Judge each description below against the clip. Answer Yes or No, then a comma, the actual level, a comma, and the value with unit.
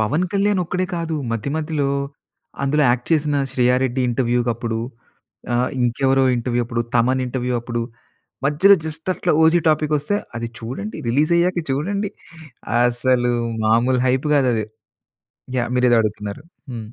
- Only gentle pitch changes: No, average, 4.4 semitones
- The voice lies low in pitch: Yes, low, 130 Hz